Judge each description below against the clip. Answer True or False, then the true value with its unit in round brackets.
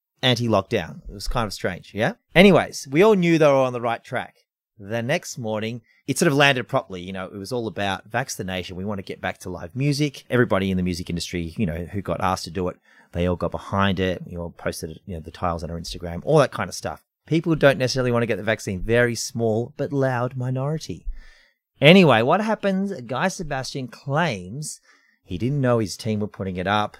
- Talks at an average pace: False (225 wpm)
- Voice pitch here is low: True (110 Hz)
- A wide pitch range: True (6.3 semitones)